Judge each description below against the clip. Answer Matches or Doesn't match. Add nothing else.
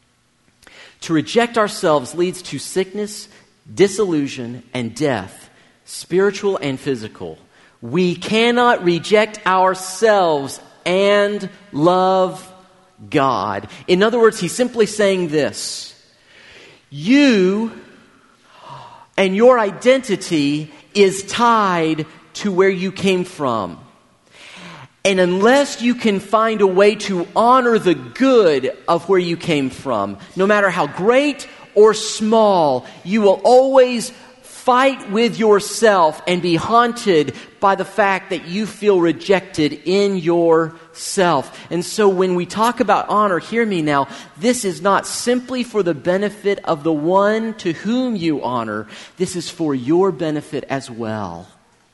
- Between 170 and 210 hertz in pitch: Matches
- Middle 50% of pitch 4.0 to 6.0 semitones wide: Matches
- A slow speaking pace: Matches